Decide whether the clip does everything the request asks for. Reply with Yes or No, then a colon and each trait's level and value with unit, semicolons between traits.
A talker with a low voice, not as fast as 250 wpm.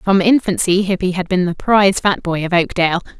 No: medium, 185 Hz; fast, 205 wpm